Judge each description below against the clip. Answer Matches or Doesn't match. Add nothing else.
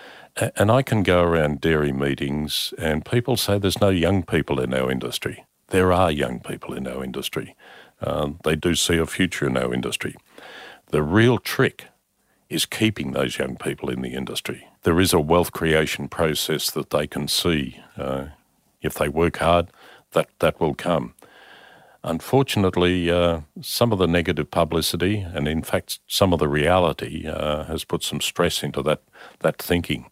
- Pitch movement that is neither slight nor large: Matches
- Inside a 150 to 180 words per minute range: Matches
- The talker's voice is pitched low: Matches